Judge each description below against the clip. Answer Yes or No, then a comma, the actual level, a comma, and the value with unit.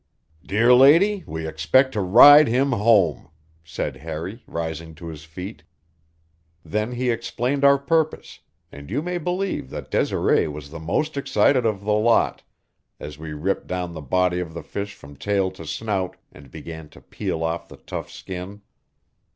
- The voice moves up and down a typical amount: No, wide, 7.5 semitones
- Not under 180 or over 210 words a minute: No, average, 165 wpm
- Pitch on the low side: Yes, very low, 95 Hz